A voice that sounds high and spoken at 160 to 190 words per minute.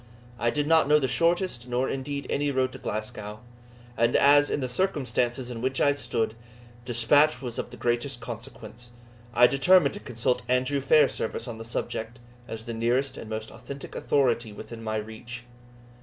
No: low, 125 Hz; average, 170 wpm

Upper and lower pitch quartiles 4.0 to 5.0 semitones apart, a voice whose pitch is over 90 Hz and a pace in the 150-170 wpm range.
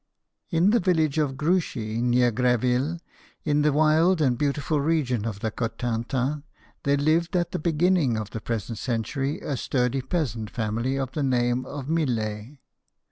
Yes: average, 4.4 semitones; low, 135 Hz; average, 155 wpm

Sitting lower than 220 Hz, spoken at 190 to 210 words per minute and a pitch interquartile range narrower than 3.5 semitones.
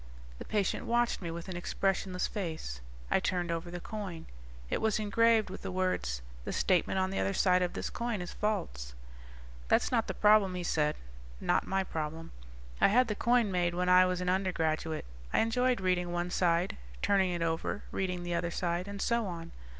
Yes: medium, 185 Hz; average, 195 wpm; average, 2.9 semitones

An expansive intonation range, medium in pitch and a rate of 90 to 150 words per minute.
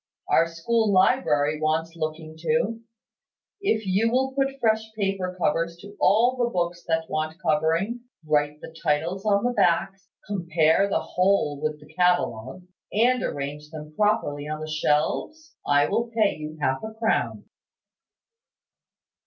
Yes: wide, 5.9 semitones; medium, 175 Hz; average, 145 wpm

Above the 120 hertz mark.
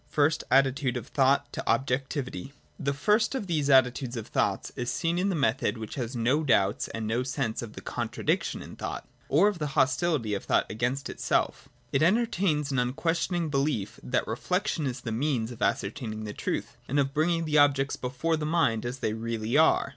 Yes: low, 135 Hz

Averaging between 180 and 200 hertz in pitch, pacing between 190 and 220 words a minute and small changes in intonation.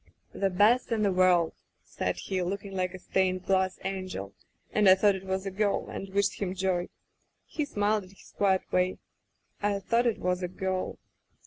Yes: high, 190 Hz; average, 200 wpm; narrow, 1.7 semitones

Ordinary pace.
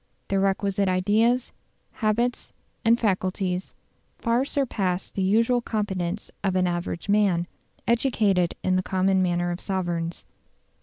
No: slow, 120 wpm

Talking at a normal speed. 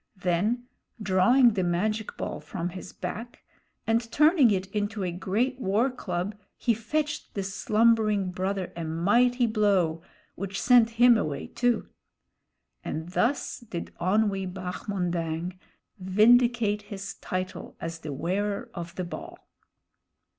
No: slow, 125 wpm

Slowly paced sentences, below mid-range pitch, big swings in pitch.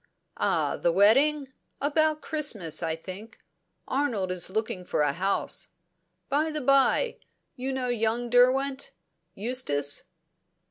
No: slow, 120 wpm; high, 245 Hz; wide, 6.7 semitones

